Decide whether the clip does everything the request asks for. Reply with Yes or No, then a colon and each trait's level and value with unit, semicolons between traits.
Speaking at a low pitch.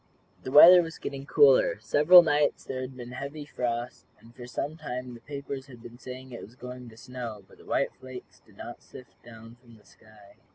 Yes: low, 125 Hz